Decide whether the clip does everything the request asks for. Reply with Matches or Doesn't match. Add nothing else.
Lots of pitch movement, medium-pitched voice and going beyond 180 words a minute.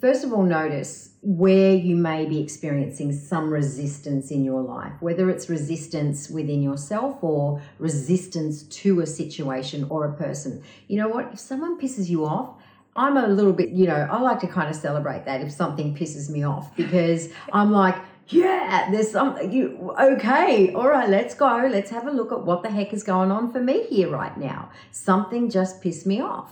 Matches